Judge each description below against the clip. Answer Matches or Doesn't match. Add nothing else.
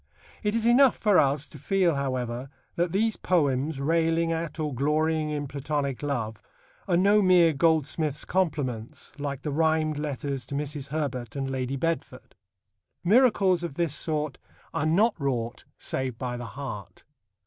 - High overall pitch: Doesn't match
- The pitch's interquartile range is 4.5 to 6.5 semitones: Doesn't match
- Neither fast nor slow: Matches